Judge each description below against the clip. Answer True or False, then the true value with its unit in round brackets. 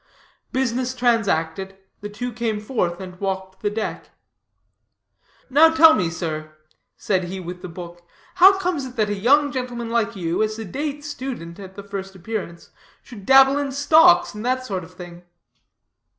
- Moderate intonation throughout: False (6.0 semitones)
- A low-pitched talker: False (210 Hz)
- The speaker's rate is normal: True (165 wpm)